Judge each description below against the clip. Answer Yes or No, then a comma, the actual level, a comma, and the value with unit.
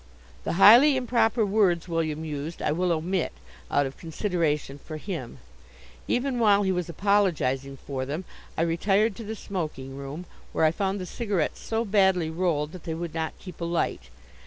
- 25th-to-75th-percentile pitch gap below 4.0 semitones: No, average, 4.6 semitones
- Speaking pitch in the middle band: Yes, medium, 175 Hz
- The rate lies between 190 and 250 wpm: No, average, 170 wpm